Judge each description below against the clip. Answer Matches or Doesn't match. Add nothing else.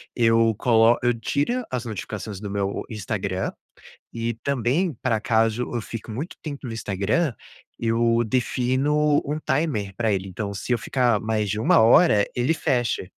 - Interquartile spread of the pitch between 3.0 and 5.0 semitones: Matches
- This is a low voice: Matches